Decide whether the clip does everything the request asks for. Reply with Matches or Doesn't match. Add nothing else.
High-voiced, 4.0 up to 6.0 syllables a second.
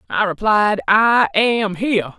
Doesn't match